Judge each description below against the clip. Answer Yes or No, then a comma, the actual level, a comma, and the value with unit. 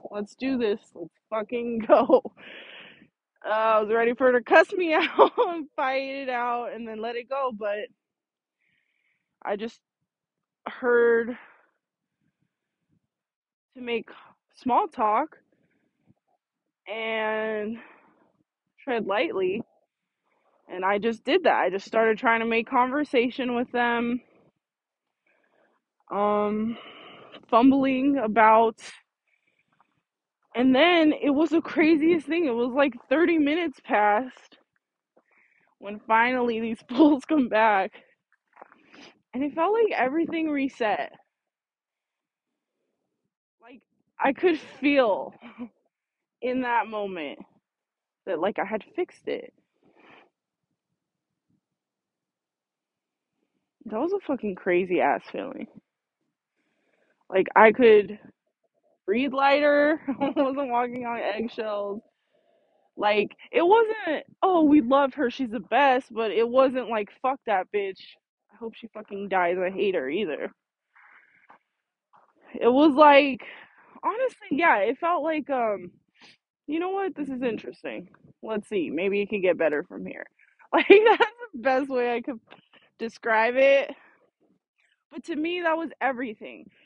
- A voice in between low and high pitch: No, very high, 250 Hz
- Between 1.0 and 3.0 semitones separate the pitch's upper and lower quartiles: No, average, 5.2 semitones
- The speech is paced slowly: Yes, slow, 120 wpm